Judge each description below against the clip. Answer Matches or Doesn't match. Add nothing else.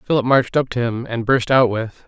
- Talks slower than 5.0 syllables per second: Doesn't match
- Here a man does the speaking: Matches